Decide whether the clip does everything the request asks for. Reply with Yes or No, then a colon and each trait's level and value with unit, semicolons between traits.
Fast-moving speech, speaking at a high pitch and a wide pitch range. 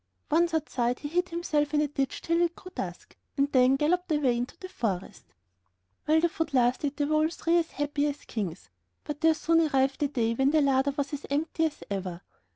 No: fast, 215 wpm; very high, 290 Hz; average, 3.3 semitones